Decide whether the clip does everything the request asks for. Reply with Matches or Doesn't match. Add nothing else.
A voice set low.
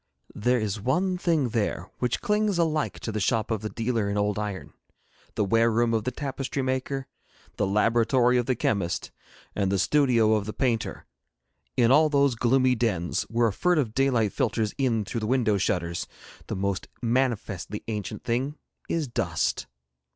Matches